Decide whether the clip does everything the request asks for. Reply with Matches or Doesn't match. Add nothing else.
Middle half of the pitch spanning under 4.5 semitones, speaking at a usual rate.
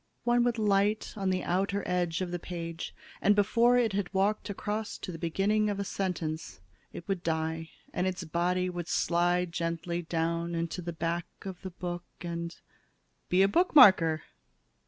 Matches